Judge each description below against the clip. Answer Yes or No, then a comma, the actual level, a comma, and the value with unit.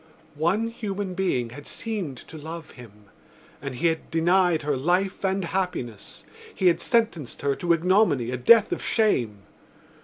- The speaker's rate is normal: Yes, average, 155 wpm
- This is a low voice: No, medium, 170 Hz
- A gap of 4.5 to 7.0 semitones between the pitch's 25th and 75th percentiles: Yes, wide, 5.5 semitones